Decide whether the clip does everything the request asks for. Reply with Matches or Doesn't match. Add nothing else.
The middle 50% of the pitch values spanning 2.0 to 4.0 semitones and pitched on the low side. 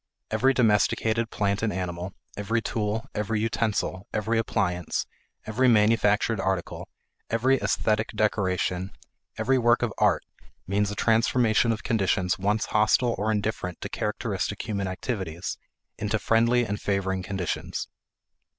Matches